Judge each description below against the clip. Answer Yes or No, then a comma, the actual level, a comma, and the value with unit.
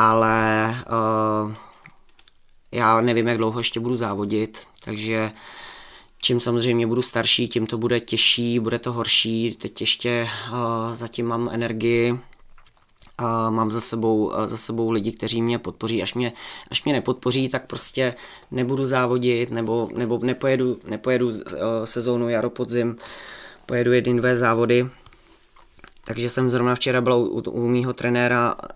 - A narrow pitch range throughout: Yes, narrow, 1.5 semitones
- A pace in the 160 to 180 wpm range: No, average, 140 wpm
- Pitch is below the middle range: Yes, low, 120 Hz